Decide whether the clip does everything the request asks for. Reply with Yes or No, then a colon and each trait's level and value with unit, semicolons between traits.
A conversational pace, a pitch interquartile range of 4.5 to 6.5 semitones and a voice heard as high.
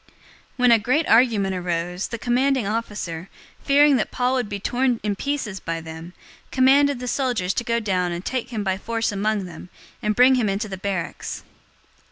Yes: average, 195 wpm; average, 4.8 semitones; high, 215 Hz